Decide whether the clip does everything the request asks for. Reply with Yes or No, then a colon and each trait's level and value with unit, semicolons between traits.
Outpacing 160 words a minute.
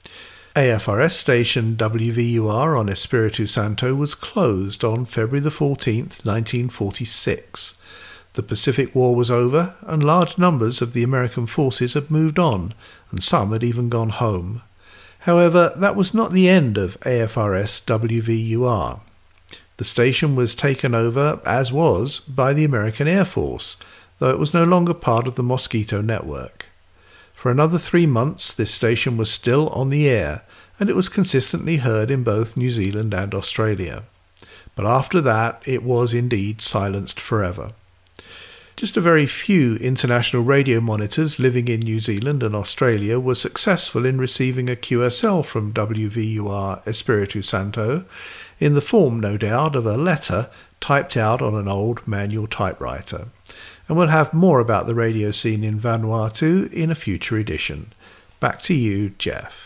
No: average, 155 wpm